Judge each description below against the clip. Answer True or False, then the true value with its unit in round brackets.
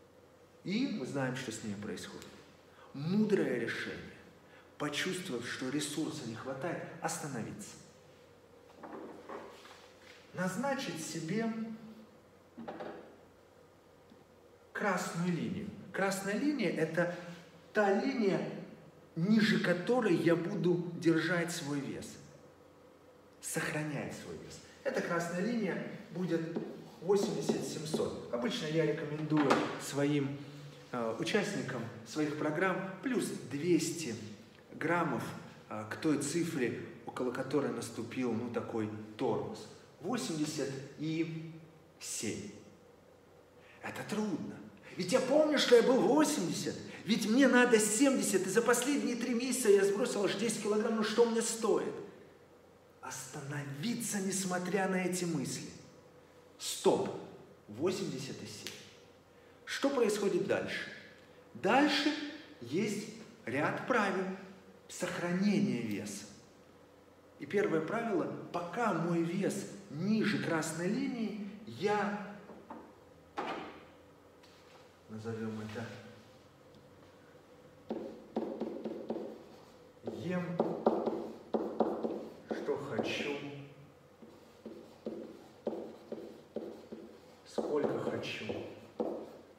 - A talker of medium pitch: True (175 Hz)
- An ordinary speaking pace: False (80 wpm)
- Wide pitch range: True (5.9 semitones)